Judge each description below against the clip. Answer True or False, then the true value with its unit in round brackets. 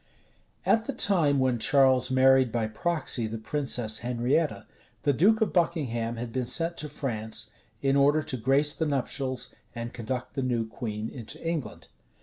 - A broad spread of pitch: False (3.9 semitones)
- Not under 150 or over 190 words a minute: True (160 wpm)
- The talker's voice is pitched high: False (130 Hz)